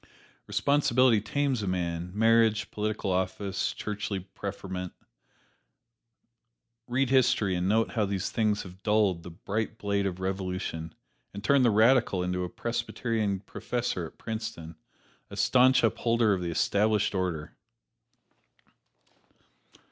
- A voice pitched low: Yes, low, 105 Hz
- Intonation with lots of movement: No, average, 3.6 semitones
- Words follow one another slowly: Yes, slow, 120 wpm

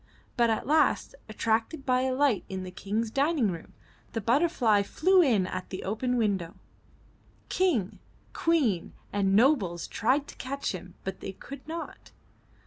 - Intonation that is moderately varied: No, wide, 6.2 semitones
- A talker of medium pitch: No, high, 230 Hz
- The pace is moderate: Yes, average, 150 wpm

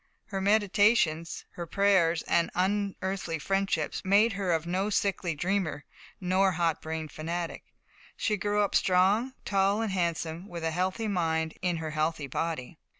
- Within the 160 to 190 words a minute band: No, average, 150 wpm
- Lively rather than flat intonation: No, average, 3.3 semitones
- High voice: No, medium, 180 Hz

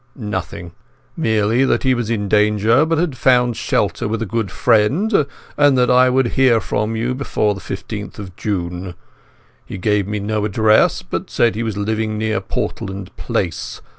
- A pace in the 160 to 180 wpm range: Yes, average, 170 wpm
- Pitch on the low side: Yes, low, 110 Hz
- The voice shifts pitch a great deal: No, average, 3.3 semitones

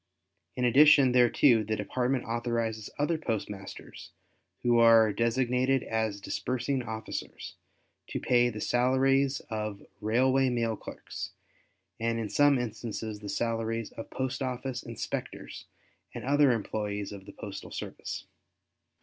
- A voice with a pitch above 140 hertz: No, low, 115 Hz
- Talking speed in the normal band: No, slow, 120 wpm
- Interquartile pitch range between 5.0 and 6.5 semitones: No, average, 2.8 semitones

